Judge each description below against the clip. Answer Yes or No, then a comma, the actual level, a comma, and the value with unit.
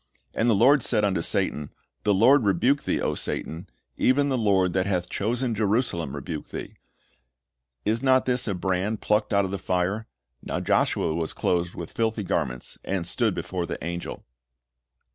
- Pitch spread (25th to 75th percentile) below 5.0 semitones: Yes, average, 4.5 semitones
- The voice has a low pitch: Yes, low, 100 Hz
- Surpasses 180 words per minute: No, average, 170 wpm